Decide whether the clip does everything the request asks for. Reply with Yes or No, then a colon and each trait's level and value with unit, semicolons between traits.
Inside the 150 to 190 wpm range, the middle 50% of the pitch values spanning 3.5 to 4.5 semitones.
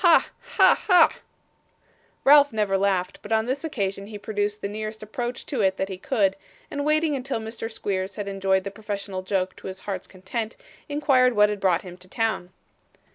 Yes: average, 185 wpm; average, 3.9 semitones